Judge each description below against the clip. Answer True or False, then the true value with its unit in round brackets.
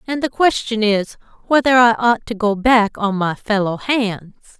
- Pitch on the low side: False (220 Hz)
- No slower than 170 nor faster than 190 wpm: True (185 wpm)